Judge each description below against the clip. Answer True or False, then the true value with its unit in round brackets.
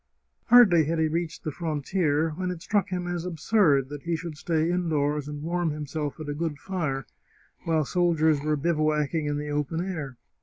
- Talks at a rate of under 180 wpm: False (185 wpm)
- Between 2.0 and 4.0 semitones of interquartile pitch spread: True (2.8 semitones)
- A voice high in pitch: False (160 Hz)